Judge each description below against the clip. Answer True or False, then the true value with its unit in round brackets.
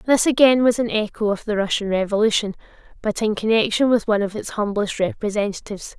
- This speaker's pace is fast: False (180 wpm)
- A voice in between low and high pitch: False (215 Hz)